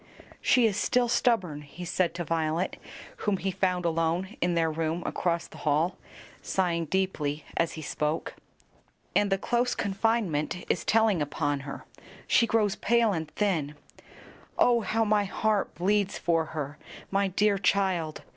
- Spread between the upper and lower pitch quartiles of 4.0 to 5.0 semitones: Yes, average, 4.3 semitones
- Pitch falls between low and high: Yes, medium, 180 Hz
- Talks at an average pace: Yes, average, 150 wpm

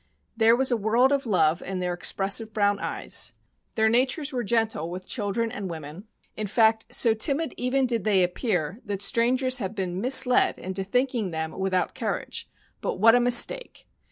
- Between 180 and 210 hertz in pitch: No, high, 220 Hz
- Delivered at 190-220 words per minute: No, average, 175 wpm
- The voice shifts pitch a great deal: No, average, 4.5 semitones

